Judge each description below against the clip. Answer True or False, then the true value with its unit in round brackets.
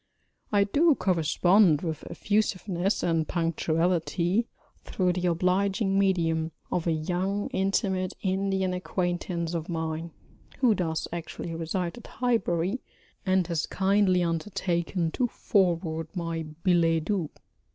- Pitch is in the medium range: True (180 Hz)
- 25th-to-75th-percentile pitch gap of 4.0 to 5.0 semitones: False (2.7 semitones)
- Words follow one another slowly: True (115 wpm)